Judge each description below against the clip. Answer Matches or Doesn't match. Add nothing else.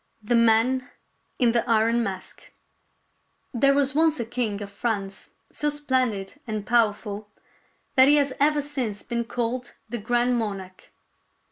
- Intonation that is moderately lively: Matches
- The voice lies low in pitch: Doesn't match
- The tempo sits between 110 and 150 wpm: Matches